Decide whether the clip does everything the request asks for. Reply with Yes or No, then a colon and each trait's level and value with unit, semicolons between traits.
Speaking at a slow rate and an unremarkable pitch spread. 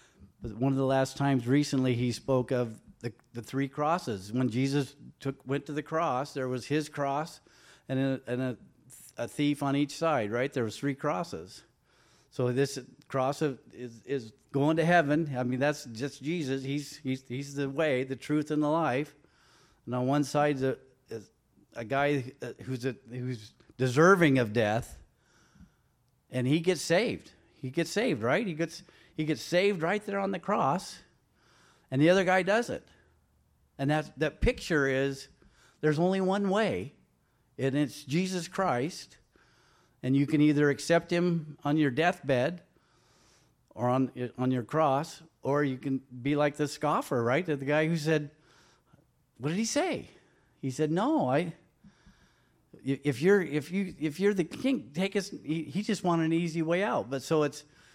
No: average, 175 wpm; average, 3.8 semitones